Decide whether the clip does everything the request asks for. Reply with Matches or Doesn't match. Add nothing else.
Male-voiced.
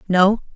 Doesn't match